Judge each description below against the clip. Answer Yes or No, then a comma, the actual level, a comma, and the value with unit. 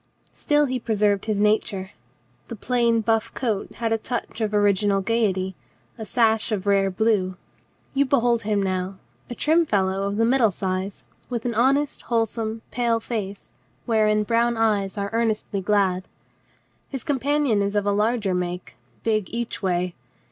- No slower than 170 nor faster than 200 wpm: No, average, 155 wpm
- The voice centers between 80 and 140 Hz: No, high, 215 Hz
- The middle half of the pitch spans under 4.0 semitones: Yes, average, 2.9 semitones